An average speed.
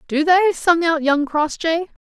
Yes: average, 175 wpm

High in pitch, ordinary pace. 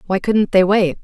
No: high, 195 Hz; fast, 235 wpm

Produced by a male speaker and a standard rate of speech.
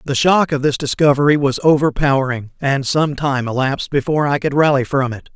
Yes: male; average, 190 wpm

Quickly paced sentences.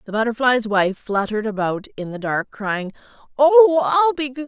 No: average, 175 wpm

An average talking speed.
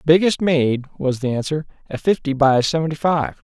Yes: average, 170 wpm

